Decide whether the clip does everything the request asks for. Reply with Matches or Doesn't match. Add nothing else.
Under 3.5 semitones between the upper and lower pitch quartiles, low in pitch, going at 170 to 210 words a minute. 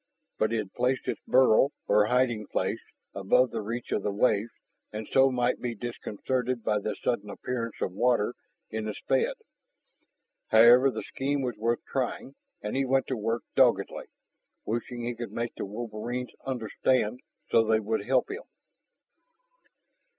Doesn't match